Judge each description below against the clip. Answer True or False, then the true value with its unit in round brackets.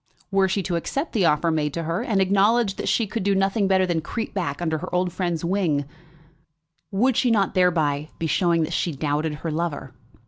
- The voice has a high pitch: False (180 Hz)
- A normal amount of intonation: True (3.6 semitones)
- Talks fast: True (210 wpm)